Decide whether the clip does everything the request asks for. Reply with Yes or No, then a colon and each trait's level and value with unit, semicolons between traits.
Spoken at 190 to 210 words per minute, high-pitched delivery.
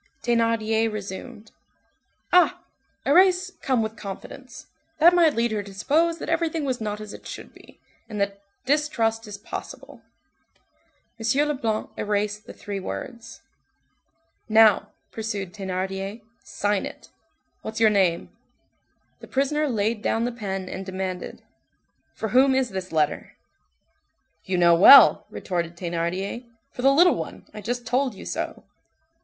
No: slow, 135 wpm; high, 220 Hz